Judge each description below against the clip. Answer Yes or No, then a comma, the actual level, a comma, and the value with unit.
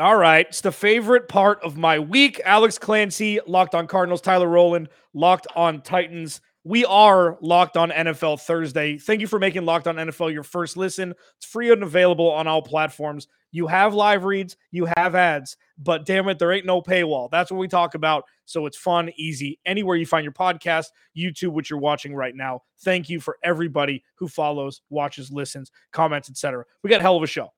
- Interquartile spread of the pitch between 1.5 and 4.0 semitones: Yes, average, 3.0 semitones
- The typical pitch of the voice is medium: Yes, medium, 170 Hz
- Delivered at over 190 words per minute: Yes, average, 200 wpm